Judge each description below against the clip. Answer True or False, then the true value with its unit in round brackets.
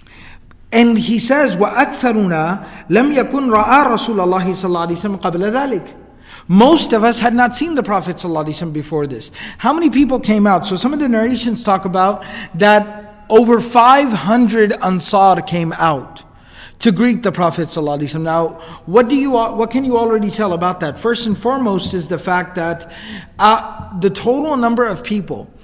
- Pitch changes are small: False (4.7 semitones)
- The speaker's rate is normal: True (145 wpm)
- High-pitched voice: True (210 Hz)